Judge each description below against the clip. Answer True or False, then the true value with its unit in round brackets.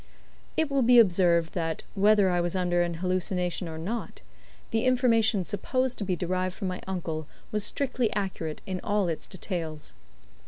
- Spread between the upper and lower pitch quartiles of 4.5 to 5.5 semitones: False (3.7 semitones)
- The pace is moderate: True (165 wpm)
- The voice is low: False (185 Hz)